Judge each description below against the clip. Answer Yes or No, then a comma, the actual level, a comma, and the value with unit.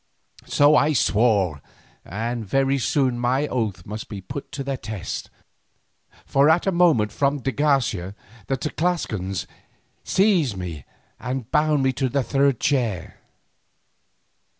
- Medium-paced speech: No, slow, 130 wpm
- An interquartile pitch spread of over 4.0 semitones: Yes, average, 5.1 semitones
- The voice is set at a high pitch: No, low, 130 Hz